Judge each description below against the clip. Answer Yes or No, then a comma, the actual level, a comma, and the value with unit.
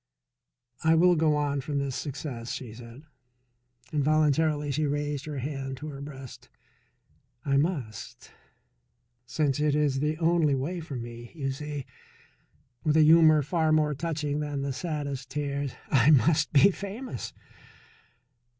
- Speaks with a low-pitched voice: No, medium, 145 Hz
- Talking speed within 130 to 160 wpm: Yes, average, 140 wpm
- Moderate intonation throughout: No, narrow, 2.2 semitones